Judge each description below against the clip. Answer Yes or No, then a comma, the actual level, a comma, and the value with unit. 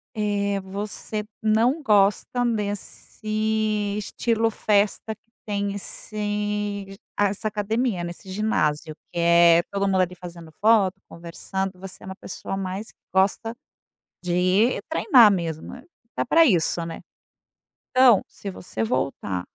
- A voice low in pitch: No, high, 200 Hz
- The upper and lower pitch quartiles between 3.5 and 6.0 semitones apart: No, average, 2.8 semitones